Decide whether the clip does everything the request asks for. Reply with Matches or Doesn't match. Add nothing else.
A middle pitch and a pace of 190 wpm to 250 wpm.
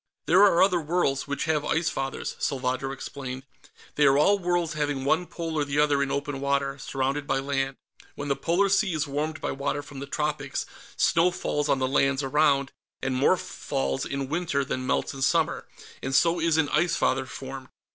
Matches